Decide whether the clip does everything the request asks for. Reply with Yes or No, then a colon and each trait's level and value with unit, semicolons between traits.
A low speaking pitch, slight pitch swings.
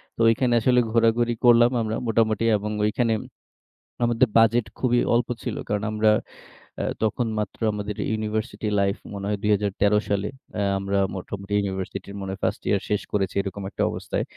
Yes: low, 105 Hz; narrow, 2.3 semitones